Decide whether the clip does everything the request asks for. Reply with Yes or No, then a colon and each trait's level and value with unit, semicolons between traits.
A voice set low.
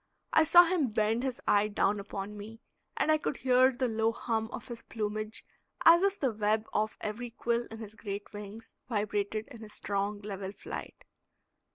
No: high, 220 Hz